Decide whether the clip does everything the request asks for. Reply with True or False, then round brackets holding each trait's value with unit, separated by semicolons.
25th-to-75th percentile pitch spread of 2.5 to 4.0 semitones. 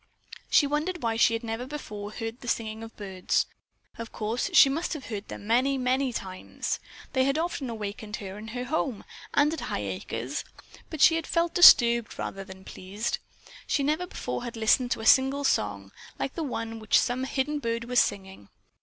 False (4.7 semitones)